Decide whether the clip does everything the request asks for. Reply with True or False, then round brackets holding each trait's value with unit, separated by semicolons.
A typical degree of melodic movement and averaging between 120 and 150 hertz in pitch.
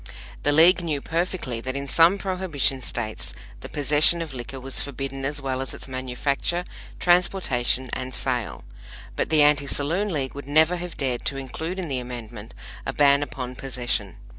True (3.9 semitones; 140 Hz)